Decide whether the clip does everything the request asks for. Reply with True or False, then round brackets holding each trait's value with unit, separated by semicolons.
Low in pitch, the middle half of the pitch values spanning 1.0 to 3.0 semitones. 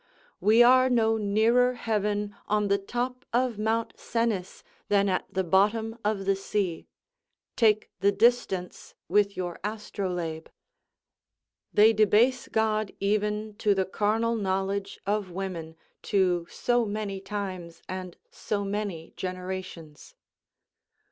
False (205 Hz; 2.6 semitones)